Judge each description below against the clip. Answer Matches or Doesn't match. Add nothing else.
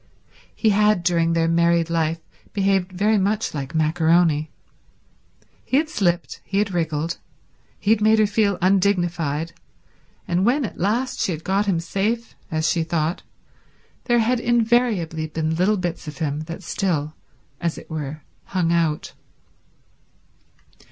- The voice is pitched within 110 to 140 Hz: Doesn't match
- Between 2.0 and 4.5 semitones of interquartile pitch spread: Matches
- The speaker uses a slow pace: Doesn't match